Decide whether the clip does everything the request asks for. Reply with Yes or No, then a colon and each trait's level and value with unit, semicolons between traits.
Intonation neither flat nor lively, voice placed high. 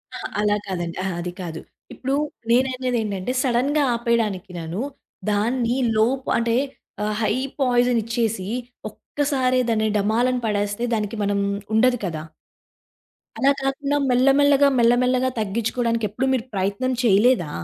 Yes: average, 3.7 semitones; high, 235 Hz